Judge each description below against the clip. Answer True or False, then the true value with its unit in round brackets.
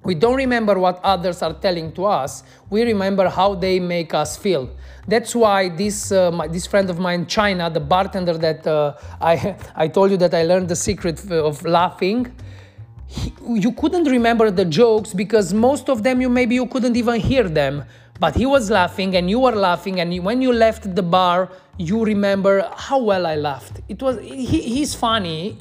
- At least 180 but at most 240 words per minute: True (200 wpm)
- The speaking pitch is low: False (195 Hz)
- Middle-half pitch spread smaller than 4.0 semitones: False (4.8 semitones)